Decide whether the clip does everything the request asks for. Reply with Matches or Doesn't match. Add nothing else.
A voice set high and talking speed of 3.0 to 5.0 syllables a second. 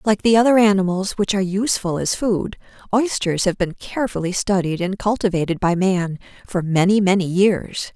Doesn't match